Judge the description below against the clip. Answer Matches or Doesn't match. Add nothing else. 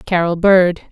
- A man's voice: Doesn't match